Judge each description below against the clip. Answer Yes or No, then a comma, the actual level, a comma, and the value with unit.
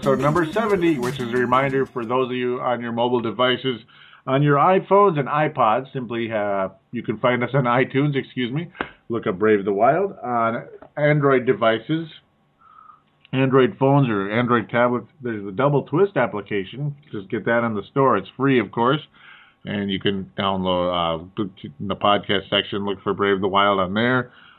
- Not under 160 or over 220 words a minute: Yes, average, 180 wpm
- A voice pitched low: Yes, low, 125 Hz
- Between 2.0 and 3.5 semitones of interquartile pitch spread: No, average, 4.3 semitones